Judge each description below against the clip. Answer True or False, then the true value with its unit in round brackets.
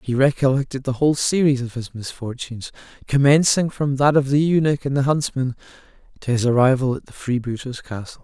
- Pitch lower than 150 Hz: True (135 Hz)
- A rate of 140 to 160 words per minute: False (180 wpm)